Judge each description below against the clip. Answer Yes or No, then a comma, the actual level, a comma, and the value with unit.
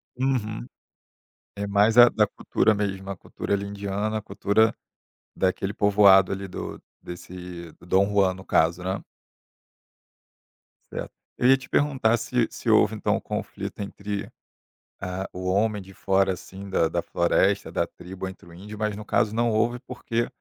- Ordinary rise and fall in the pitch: No, narrow, 2.3 semitones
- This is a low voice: Yes, low, 100 Hz